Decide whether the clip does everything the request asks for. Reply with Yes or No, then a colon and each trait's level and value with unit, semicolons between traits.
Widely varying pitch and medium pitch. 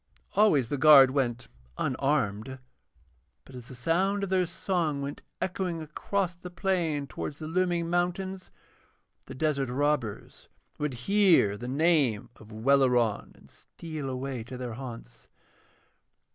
Yes: wide, 5.7 semitones; medium, 145 Hz